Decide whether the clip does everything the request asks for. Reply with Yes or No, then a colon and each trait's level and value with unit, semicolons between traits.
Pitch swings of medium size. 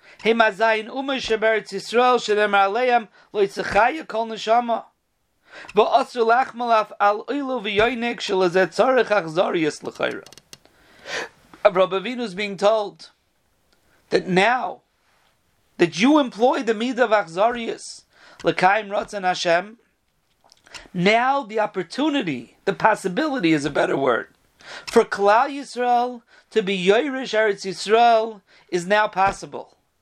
Yes: average, 3.4 semitones